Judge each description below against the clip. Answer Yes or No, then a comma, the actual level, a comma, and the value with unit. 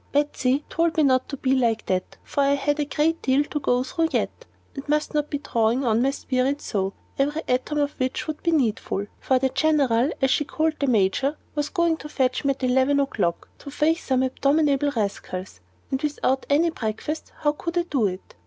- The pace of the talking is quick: Yes, fast, 210 wpm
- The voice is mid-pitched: No, very high, 275 Hz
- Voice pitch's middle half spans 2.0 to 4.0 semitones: Yes, average, 2.9 semitones